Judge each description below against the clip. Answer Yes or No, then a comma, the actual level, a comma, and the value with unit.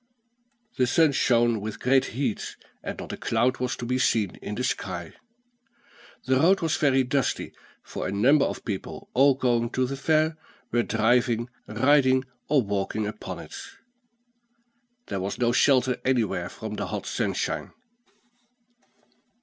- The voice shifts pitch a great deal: No, average, 3.1 semitones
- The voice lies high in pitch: No, low, 125 Hz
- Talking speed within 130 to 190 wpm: Yes, average, 150 wpm